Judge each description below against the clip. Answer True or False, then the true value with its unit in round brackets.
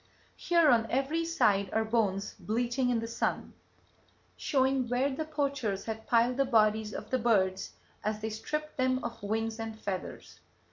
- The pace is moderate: True (160 wpm)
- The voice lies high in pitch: True (230 Hz)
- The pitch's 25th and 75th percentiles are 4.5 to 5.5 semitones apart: False (3.4 semitones)